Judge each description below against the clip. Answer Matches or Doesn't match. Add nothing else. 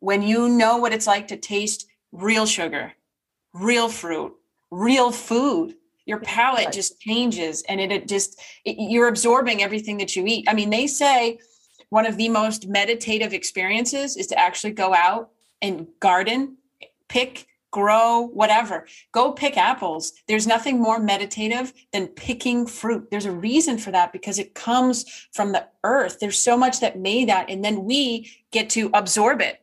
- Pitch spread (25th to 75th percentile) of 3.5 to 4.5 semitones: Doesn't match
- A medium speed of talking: Matches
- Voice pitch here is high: Matches